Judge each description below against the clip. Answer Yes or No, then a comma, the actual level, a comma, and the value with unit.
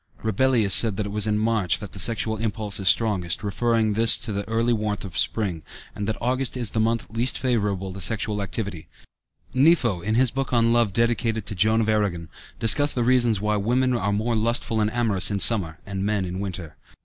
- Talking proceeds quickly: Yes, fast, 225 wpm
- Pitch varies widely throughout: No, narrow, 2.6 semitones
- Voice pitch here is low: Yes, low, 110 Hz